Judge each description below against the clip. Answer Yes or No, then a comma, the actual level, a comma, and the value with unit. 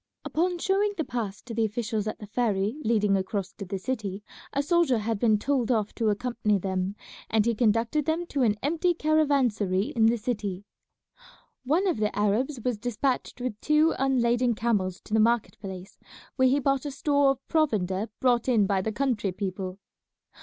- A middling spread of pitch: Yes, average, 4.7 semitones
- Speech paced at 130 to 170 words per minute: No, average, 180 wpm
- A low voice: No, high, 230 Hz